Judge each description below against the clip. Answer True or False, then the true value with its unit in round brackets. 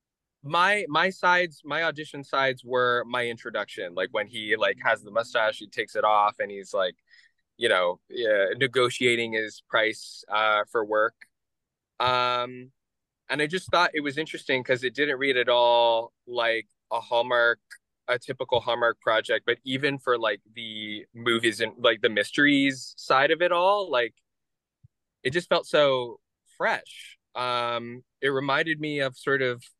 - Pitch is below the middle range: True (125 Hz)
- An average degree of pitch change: True (3.9 semitones)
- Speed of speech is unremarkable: True (160 wpm)